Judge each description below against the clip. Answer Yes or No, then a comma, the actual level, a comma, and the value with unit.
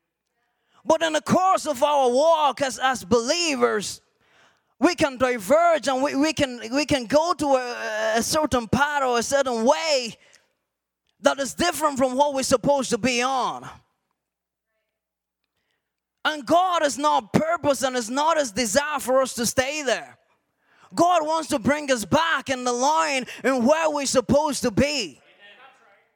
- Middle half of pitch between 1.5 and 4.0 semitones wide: Yes, average, 3.1 semitones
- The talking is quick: No, average, 160 wpm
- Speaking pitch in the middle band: No, very high, 280 Hz